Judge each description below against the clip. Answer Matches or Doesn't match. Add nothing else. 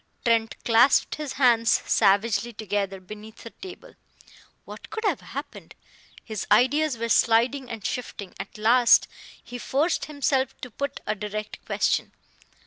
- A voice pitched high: Matches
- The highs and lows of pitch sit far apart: Doesn't match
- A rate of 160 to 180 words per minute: Doesn't match